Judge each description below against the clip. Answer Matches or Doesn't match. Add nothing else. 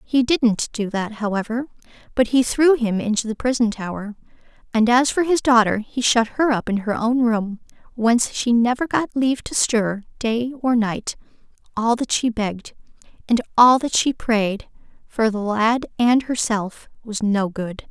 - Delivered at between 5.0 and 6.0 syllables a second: Doesn't match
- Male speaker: Doesn't match